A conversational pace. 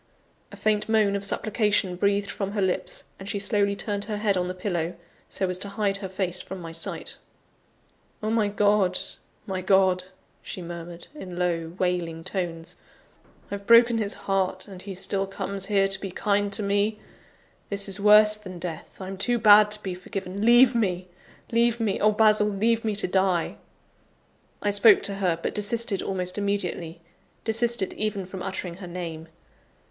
Yes: average, 175 wpm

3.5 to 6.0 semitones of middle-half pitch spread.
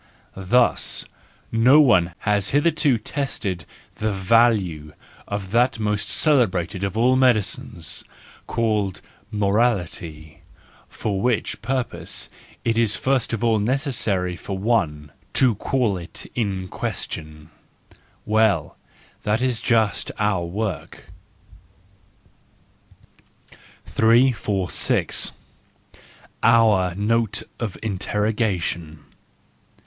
Yes: average, 3.9 semitones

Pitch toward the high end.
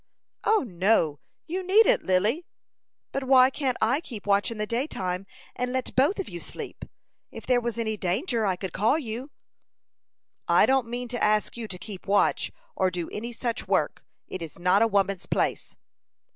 Yes: high, 225 Hz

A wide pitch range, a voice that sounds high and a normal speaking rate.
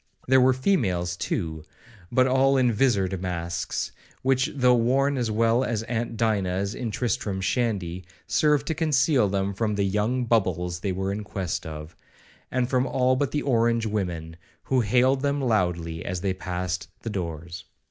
No: wide, 5.7 semitones; low, 110 Hz; average, 165 wpm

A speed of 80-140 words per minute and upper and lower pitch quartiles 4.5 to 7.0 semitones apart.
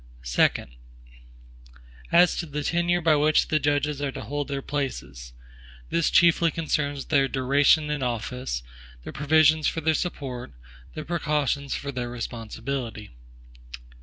No: slow, 135 wpm; average, 3.5 semitones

